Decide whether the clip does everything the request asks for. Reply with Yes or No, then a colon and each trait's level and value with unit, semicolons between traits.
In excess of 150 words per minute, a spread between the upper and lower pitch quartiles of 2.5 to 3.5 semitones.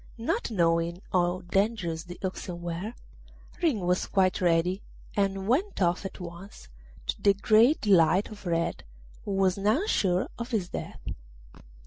No: average, 145 wpm; average, 3.1 semitones